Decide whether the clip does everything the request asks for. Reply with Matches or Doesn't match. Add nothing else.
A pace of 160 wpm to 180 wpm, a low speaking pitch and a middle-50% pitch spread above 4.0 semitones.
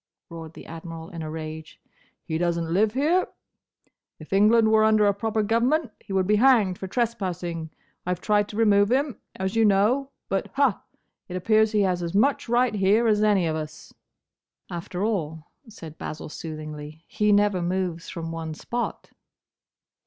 Doesn't match